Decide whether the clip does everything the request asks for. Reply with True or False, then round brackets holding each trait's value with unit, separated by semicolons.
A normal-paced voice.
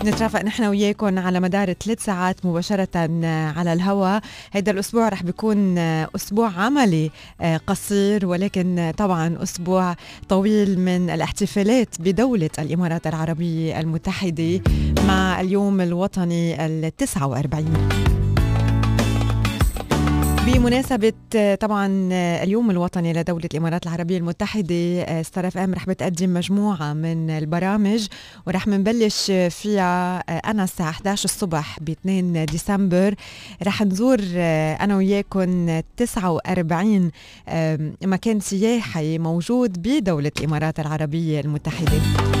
True (95 wpm)